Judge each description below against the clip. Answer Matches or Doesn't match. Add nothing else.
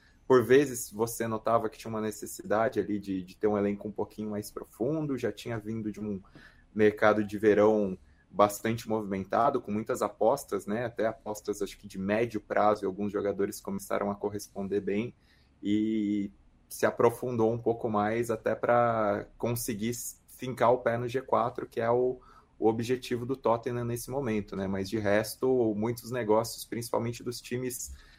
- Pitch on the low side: Matches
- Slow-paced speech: Doesn't match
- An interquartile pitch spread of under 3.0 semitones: Matches